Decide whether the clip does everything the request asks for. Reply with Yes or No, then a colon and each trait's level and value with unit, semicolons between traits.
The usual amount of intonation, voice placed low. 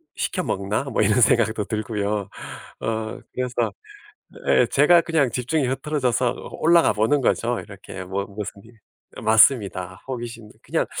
Yes: average, 4.0 semitones; low, 115 Hz